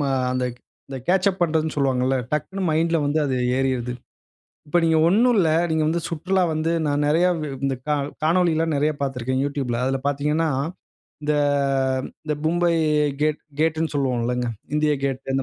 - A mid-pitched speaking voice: Yes, medium, 150 Hz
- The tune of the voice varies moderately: Yes, average, 3.5 semitones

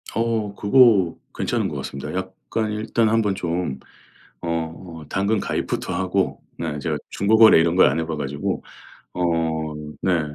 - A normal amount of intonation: Yes, average, 4.7 semitones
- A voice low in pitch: Yes, very low, 95 Hz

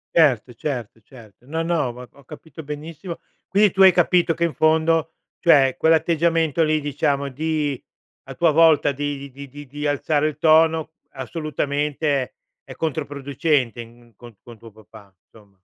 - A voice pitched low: No, medium, 145 Hz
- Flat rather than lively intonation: No, average, 3.6 semitones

